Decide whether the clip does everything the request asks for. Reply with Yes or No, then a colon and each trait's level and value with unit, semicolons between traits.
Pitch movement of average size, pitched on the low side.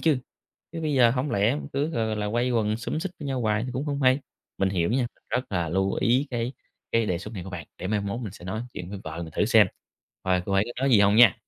Yes: average, 4.6 semitones; low, 110 Hz